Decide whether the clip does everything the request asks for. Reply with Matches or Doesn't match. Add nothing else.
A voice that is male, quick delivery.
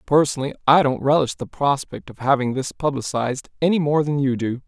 Doesn't match